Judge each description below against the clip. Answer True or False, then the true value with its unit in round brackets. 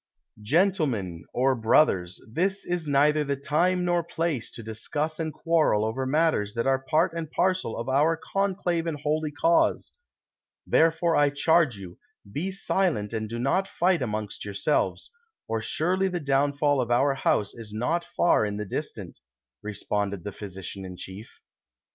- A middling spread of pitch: False (7.2 semitones)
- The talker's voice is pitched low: False (145 Hz)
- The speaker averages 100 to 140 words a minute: False (155 wpm)